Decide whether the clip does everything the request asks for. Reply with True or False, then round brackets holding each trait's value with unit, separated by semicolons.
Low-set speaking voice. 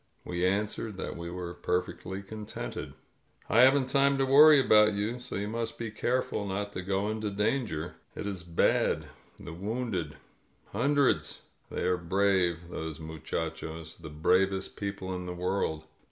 True (100 Hz)